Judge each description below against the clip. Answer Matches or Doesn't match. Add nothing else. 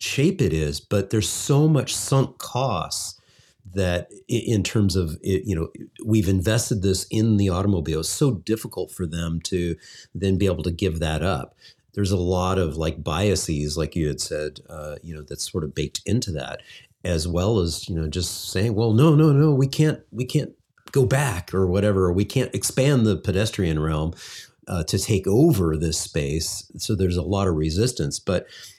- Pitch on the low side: Matches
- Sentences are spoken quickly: Doesn't match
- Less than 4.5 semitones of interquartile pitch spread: Doesn't match